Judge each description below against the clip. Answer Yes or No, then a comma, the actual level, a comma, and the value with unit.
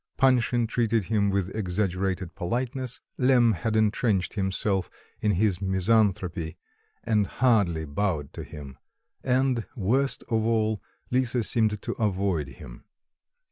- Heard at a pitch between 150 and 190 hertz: No, low, 105 Hz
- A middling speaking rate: No, slow, 120 wpm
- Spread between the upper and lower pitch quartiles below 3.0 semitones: No, average, 4.1 semitones